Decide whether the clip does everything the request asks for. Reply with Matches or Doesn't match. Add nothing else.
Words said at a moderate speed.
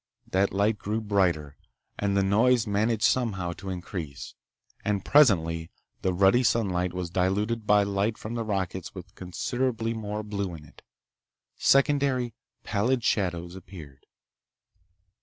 Doesn't match